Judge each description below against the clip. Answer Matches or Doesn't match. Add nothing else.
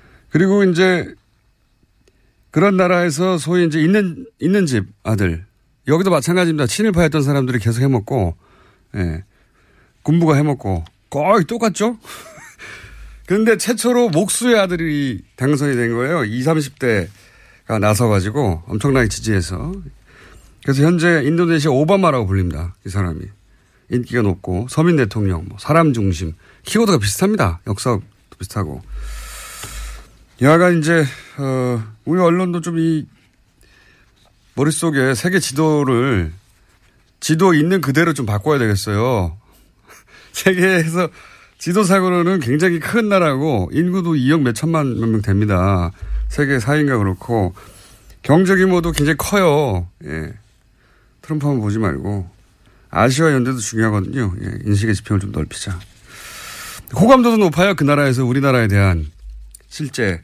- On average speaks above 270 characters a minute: Matches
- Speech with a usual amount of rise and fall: Doesn't match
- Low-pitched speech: Matches